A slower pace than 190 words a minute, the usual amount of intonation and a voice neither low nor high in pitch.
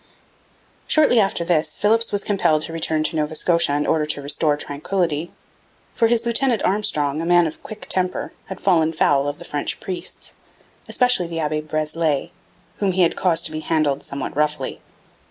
Yes: average, 175 wpm; average, 4.0 semitones; medium, 165 Hz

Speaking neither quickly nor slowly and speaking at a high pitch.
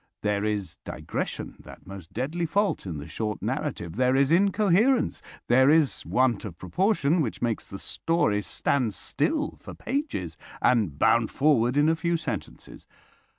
No: average, 150 wpm; low, 130 Hz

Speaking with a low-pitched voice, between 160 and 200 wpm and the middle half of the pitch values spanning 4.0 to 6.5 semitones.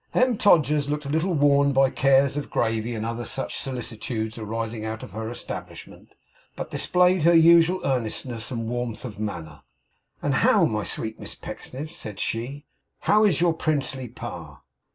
Yes: low, 130 Hz; average, 165 wpm; average, 5.3 semitones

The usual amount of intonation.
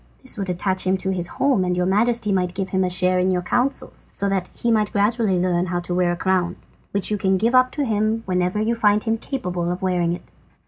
Yes: average, 3.1 semitones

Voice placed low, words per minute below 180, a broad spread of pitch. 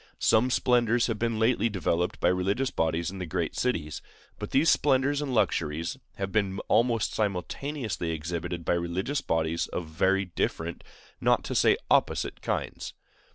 Yes: very low, 95 Hz; average, 155 wpm; wide, 5.7 semitones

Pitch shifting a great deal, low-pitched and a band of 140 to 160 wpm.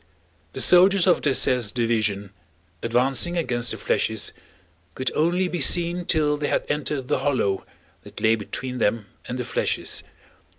Yes: wide, 6.2 semitones; low, 130 Hz; average, 145 wpm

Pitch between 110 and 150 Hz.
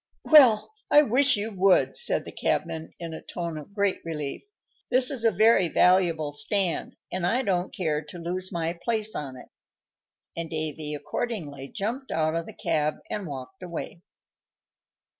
No: medium, 180 Hz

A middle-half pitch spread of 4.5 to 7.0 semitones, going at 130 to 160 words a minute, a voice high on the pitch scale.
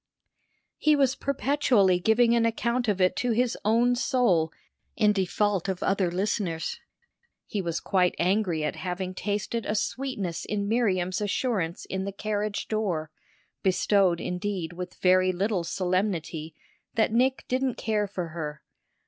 No: average, 4.0 semitones; average, 140 wpm; high, 200 Hz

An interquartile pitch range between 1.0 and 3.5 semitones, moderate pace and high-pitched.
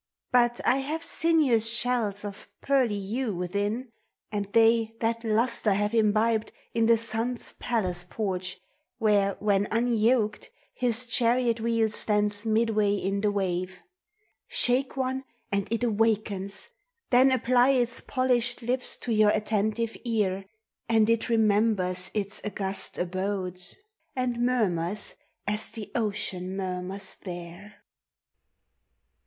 No: average, 3.0 semitones; slow, 120 wpm; high, 220 Hz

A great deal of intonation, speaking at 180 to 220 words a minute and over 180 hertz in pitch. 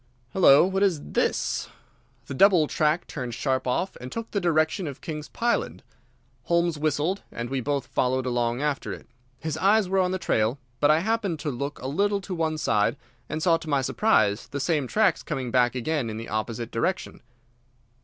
No: wide, 5.9 semitones; average, 190 wpm; medium, 150 Hz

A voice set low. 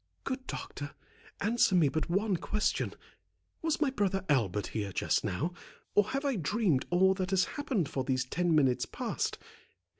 No: medium, 185 Hz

